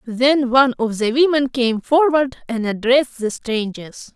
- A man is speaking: No, female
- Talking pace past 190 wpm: No, average, 160 wpm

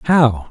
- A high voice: No, low, 130 Hz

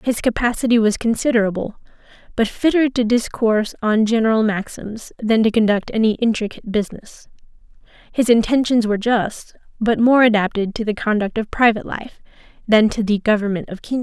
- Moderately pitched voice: No, high, 220 Hz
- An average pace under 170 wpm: Yes, average, 155 wpm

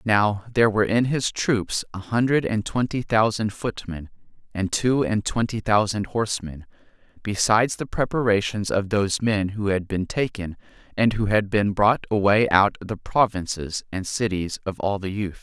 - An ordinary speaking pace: Yes, average, 170 wpm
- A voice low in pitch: Yes, low, 105 Hz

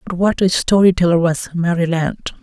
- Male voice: Yes, male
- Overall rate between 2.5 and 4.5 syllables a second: No, 4.9 syllables/s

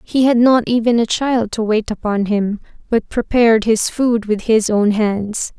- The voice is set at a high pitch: Yes, high, 225 Hz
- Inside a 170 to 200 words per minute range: Yes, average, 195 wpm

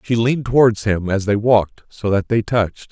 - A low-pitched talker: Yes, low, 110 Hz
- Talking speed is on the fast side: Yes, fast, 225 wpm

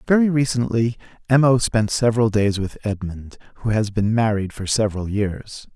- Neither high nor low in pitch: No, low, 110 Hz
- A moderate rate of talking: Yes, average, 165 wpm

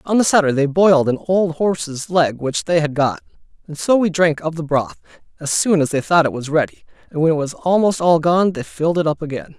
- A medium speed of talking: No, fast, 250 wpm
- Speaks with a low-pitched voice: No, medium, 160 Hz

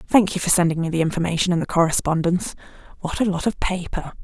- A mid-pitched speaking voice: Yes, medium, 175 Hz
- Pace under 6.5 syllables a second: No, 6.8 syllables/s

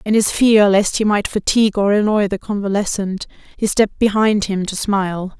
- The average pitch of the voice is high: Yes, high, 205 Hz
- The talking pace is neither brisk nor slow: Yes, average, 190 wpm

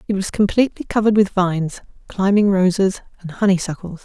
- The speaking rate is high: No, average, 150 wpm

